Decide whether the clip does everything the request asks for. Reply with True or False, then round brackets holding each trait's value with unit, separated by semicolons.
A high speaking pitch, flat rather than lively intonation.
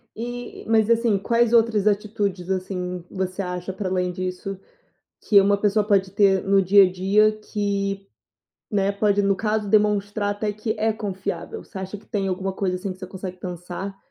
True (200 Hz; 2.0 semitones)